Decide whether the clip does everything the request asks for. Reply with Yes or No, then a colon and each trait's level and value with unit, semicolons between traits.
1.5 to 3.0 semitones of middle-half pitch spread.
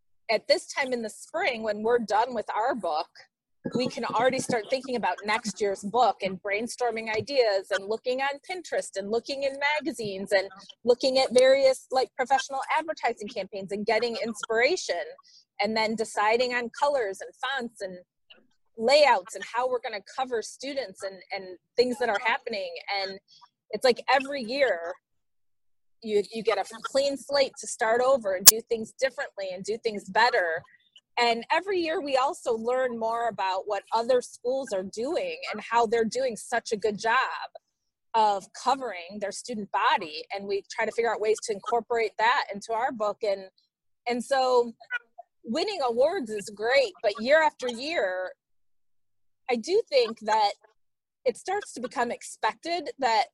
No: average, 4.6 semitones